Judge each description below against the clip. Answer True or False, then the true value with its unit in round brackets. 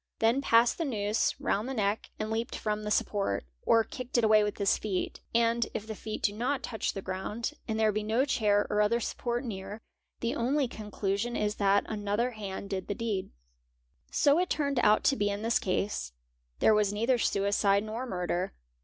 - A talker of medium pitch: False (215 Hz)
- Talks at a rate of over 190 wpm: True (200 wpm)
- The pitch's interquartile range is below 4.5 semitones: True (2.5 semitones)